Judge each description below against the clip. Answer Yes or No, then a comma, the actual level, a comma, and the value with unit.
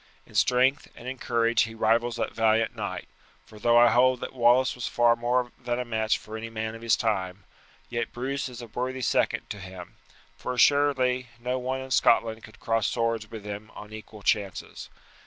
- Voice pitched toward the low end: Yes, low, 120 Hz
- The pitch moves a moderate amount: No, narrow, 2.2 semitones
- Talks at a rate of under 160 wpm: No, average, 195 wpm